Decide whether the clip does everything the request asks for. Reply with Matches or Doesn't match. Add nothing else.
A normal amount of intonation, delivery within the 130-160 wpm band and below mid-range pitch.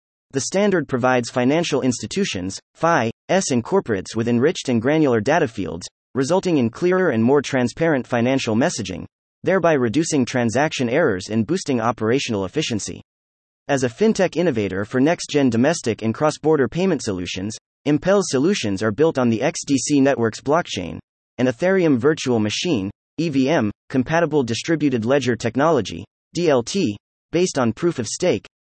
Doesn't match